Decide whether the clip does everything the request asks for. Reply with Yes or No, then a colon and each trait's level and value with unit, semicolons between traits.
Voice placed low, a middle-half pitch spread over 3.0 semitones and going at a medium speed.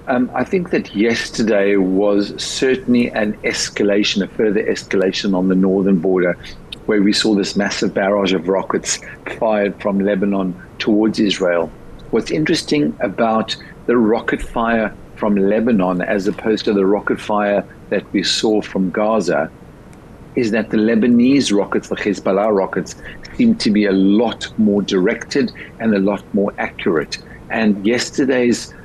No: low, 105 Hz; narrow, 2.6 semitones; average, 145 wpm